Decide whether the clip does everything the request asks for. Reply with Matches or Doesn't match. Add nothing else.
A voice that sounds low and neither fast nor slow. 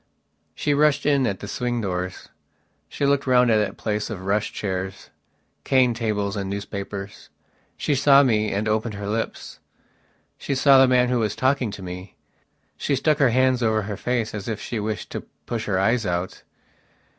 Matches